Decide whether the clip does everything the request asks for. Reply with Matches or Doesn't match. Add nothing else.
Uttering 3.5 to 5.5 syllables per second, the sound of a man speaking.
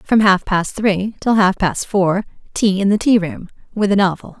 Doesn't match